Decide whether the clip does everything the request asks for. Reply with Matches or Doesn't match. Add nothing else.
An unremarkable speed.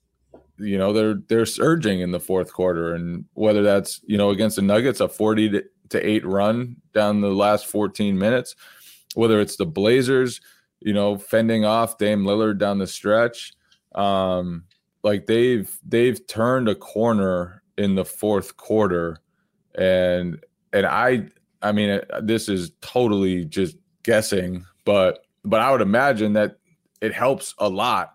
Matches